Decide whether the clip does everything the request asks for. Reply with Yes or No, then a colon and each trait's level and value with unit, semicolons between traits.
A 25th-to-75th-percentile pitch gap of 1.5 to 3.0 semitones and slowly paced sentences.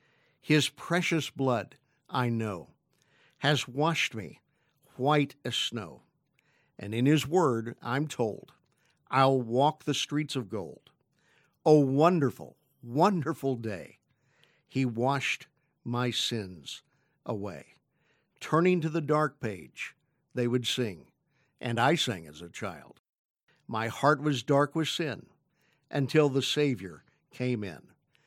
No: average, 4.0 semitones; slow, 120 wpm